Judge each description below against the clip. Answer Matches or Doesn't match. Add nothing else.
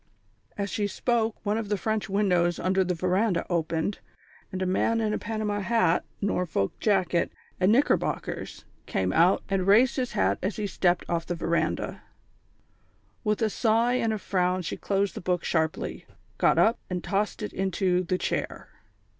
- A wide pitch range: Doesn't match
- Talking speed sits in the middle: Matches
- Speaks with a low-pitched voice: Doesn't match